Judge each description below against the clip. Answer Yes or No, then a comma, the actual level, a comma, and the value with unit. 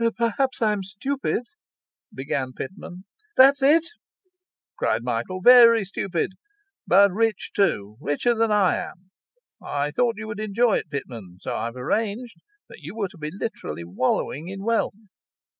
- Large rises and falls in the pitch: Yes, wide, 7.8 semitones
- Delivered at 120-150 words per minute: Yes, average, 145 wpm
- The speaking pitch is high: Yes, high, 195 Hz